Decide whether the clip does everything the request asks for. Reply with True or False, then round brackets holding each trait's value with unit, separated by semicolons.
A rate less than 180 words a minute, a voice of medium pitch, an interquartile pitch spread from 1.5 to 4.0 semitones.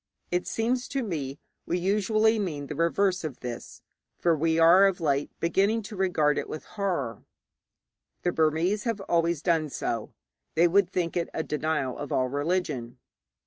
False (165 wpm; 170 Hz; 4.5 semitones)